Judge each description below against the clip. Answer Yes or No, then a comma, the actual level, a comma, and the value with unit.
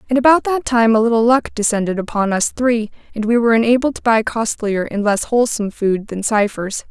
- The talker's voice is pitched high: Yes, high, 225 Hz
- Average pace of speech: No, fast, 210 wpm